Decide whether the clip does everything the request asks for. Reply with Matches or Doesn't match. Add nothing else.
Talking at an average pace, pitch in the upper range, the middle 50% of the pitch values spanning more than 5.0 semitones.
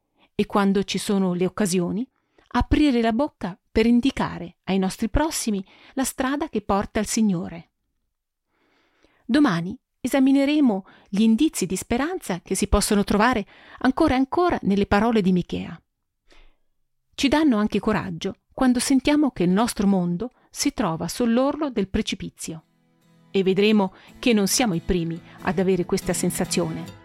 Matches